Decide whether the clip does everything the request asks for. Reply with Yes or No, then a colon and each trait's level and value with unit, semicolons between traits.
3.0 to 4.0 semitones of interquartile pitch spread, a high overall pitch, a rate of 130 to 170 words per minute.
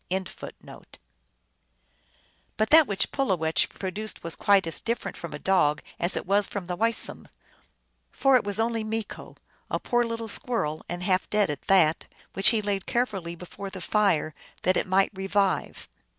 Yes: average, 3.4 semitones; high, 195 Hz; average, 155 wpm